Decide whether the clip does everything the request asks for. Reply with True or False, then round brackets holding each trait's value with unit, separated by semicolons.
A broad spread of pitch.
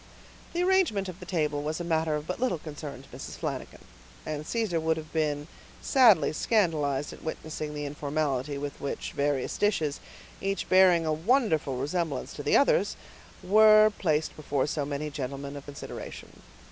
False (4.1 semitones)